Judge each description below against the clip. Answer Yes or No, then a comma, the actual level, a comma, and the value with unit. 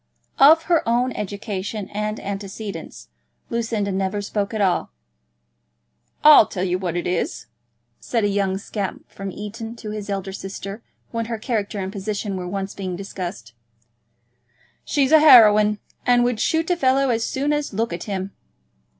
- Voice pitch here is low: No, high, 210 Hz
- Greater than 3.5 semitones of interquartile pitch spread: No, average, 3.2 semitones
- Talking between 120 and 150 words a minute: No, average, 160 wpm